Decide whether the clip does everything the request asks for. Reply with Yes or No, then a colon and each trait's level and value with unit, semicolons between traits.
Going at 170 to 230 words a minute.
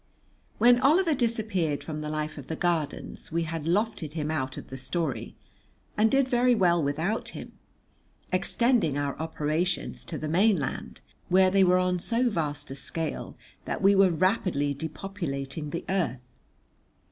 No: average, 155 wpm